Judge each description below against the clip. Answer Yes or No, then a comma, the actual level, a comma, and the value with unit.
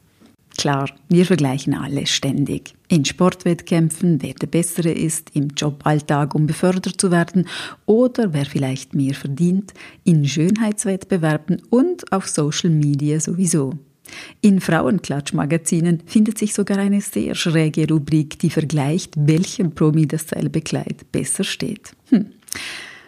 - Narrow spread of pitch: No, average, 4.3 semitones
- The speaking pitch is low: No, medium, 165 Hz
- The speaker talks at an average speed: No, slow, 120 wpm